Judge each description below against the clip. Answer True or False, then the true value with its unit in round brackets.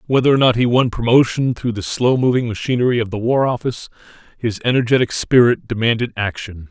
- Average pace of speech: True (180 wpm)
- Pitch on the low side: True (120 Hz)